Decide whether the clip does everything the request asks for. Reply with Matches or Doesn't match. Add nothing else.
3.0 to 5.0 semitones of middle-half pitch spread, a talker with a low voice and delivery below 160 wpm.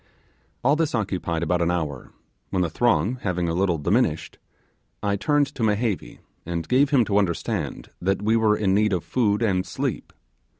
Doesn't match